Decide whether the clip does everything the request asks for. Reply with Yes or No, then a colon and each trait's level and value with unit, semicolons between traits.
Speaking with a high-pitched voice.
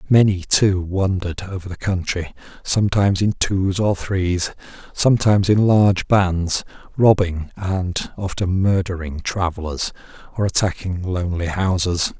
No: very low, 95 Hz